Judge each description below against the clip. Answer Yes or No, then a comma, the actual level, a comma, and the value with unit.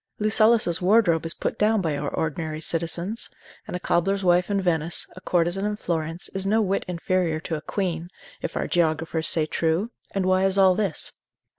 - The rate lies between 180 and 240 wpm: Yes, average, 185 wpm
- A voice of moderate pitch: Yes, medium, 175 Hz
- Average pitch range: Yes, average, 3.2 semitones